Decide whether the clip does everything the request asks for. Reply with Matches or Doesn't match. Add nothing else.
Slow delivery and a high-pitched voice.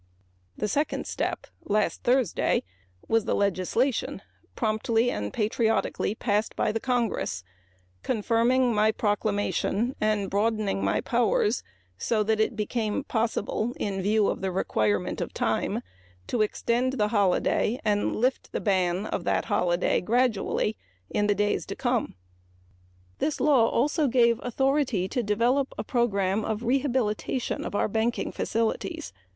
Matches